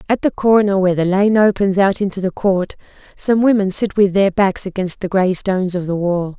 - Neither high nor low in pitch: No, high, 195 Hz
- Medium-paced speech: No, fast, 225 wpm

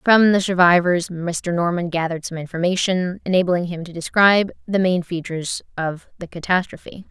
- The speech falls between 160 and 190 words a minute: No, average, 150 wpm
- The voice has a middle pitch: Yes, medium, 175 Hz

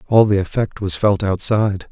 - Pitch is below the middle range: Yes, low, 100 Hz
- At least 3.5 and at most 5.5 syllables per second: Yes, 5.3 syllables/s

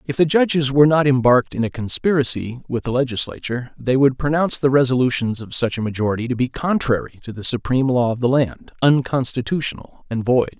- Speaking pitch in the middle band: No, low, 130 Hz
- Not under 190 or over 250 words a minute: Yes, average, 195 wpm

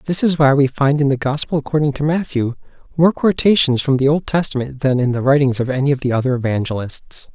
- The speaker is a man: Yes, male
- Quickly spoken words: Yes, fast, 220 wpm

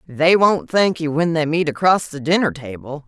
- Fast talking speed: Yes, fast, 215 wpm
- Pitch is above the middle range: No, medium, 160 Hz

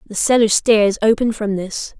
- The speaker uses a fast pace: No, average, 180 wpm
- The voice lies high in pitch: Yes, high, 215 Hz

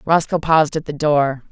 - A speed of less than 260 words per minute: Yes, average, 200 wpm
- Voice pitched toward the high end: No, medium, 150 Hz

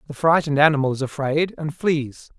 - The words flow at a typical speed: Yes, average, 175 wpm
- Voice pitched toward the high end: No, medium, 150 Hz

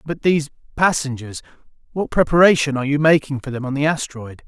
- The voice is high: No, medium, 145 Hz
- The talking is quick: No, average, 160 wpm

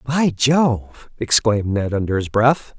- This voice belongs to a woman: No, male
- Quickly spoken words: No, average, 150 wpm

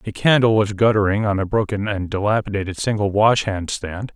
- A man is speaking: Yes, male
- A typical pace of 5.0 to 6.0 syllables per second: Yes, 5.5 syllables/s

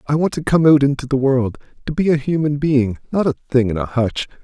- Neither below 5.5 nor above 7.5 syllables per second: Yes, 6.1 syllables/s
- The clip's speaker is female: No, male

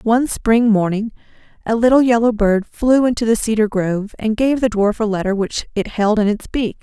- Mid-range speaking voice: No, high, 220 Hz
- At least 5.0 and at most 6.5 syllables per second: Yes, 5.3 syllables/s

